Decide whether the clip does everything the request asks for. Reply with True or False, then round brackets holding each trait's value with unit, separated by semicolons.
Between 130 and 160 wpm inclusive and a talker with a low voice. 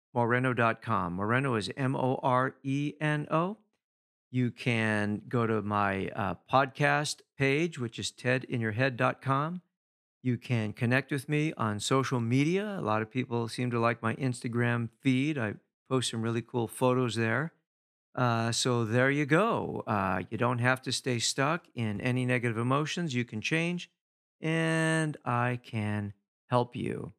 True (150 wpm; 125 Hz)